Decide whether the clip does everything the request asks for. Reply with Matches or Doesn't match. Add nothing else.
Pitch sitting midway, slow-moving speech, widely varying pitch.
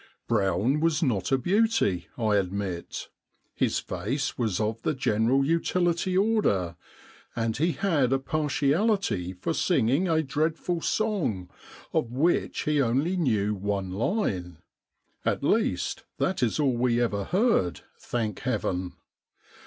Doesn't match